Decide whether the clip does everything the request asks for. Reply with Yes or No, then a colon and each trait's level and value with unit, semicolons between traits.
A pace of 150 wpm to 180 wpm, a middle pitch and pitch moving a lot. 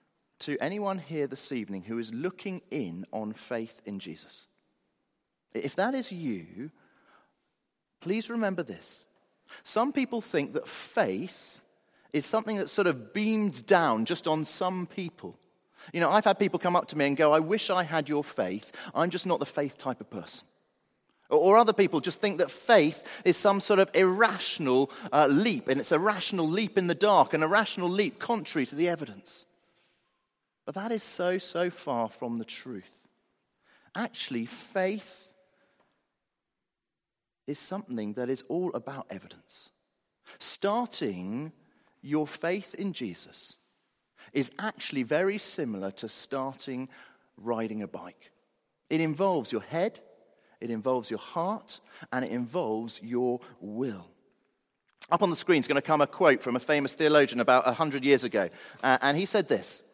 Yes: average, 155 wpm; medium, 165 Hz; wide, 7.5 semitones